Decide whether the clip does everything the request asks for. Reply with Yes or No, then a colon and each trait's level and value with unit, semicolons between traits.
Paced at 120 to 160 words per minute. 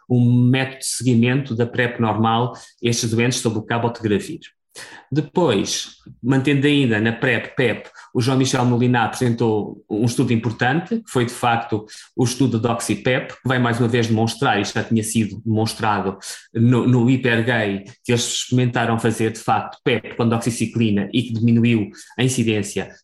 No: average, 170 wpm